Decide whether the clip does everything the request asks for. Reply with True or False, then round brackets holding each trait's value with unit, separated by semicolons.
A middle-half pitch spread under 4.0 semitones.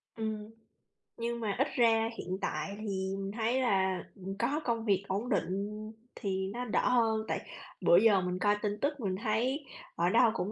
True (3.2 semitones)